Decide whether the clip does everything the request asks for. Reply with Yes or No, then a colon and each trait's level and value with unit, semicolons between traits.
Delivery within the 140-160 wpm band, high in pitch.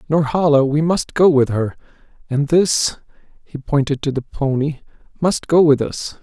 No: average, 145 wpm; medium, 145 Hz